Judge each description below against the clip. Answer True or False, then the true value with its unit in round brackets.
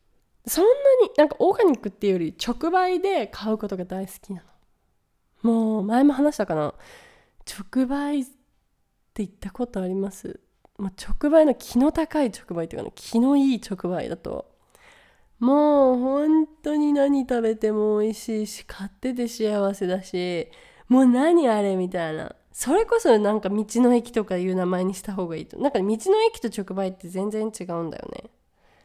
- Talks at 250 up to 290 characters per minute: False (320 characters per minute)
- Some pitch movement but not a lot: False (6.4 semitones)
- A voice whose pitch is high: True (220 Hz)